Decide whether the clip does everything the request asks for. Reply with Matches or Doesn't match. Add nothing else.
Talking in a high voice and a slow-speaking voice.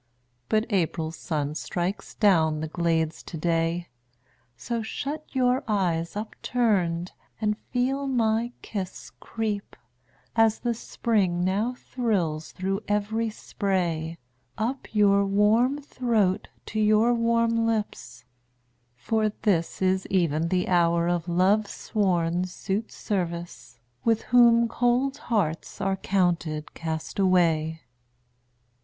Matches